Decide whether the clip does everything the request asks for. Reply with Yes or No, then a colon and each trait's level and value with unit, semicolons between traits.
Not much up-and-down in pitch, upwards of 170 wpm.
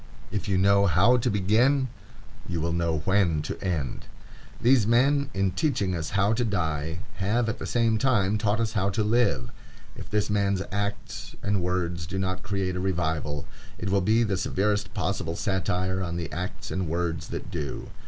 No: average, 3.5 semitones; average, 185 wpm